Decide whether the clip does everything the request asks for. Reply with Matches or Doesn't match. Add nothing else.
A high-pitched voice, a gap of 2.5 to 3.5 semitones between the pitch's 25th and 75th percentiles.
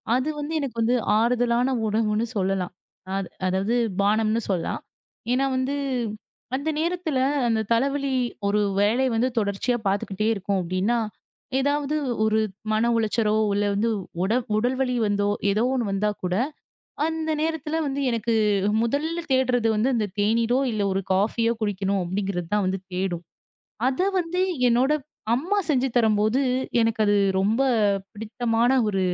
Doesn't match